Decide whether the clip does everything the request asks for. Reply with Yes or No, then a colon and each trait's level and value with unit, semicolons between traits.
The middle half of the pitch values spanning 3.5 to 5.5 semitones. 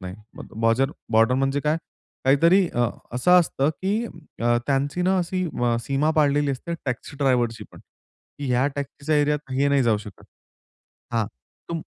Yes: average, 3.9 semitones